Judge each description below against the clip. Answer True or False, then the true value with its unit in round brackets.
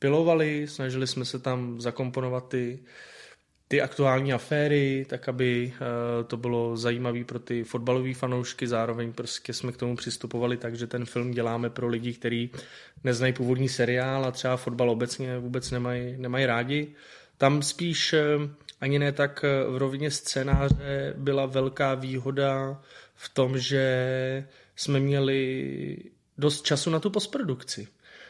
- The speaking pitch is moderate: False (130 Hz)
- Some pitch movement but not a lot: False (2.2 semitones)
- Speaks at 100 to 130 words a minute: False (140 wpm)